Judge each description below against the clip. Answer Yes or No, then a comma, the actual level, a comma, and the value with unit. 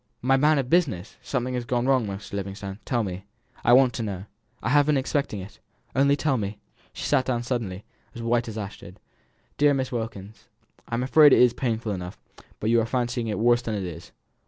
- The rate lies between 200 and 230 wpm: Yes, fast, 205 wpm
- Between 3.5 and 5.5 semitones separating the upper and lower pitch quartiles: Yes, average, 4.1 semitones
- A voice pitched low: Yes, low, 120 Hz